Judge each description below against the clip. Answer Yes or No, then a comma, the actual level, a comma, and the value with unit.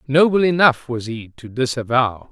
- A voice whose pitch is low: Yes, low, 130 Hz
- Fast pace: No, average, 155 wpm